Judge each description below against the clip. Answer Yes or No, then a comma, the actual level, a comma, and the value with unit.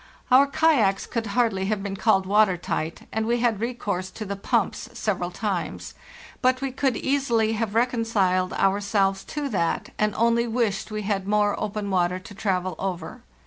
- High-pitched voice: Yes, high, 210 Hz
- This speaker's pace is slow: No, average, 170 wpm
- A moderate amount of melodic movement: Yes, average, 3.3 semitones